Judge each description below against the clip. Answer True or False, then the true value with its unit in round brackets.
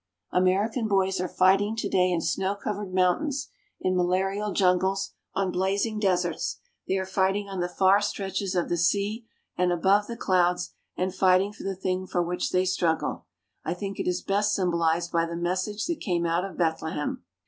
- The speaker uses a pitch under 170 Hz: False (185 Hz)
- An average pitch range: False (2.0 semitones)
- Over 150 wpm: True (180 wpm)